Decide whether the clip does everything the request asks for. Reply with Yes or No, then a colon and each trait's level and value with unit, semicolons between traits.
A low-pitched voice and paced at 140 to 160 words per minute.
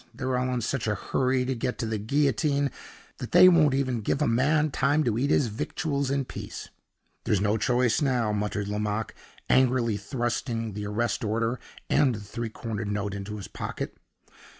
No: low, 120 Hz; average, 180 wpm